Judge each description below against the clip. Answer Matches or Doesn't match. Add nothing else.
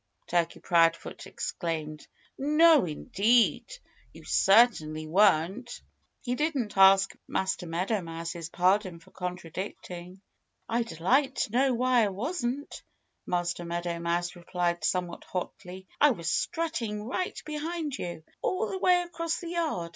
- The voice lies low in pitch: Doesn't match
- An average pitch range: Doesn't match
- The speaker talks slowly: Matches